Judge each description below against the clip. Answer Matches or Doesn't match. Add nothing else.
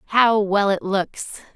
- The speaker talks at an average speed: Matches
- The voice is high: Matches